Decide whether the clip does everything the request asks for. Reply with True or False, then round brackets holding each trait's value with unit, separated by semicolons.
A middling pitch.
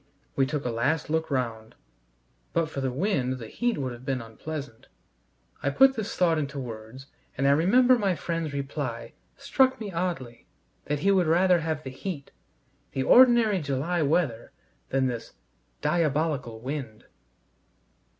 True (145 Hz)